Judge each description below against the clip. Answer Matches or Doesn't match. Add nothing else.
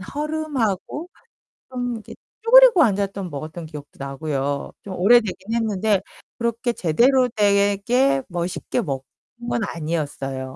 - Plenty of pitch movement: Matches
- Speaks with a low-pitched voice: Doesn't match